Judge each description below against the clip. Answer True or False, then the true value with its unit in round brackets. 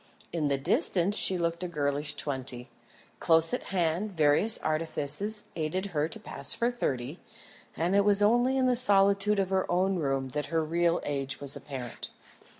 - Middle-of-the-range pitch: True (170 Hz)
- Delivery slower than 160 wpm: False (170 wpm)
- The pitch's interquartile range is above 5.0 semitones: True (5.5 semitones)